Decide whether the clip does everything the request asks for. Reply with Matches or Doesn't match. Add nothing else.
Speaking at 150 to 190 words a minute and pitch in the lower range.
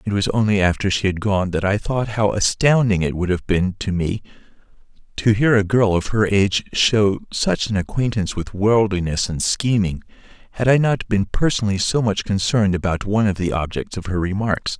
Doesn't match